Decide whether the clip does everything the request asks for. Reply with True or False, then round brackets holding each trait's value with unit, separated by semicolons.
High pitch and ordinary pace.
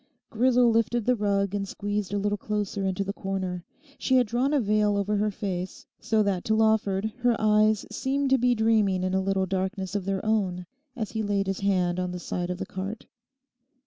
False (205 Hz; 210 wpm)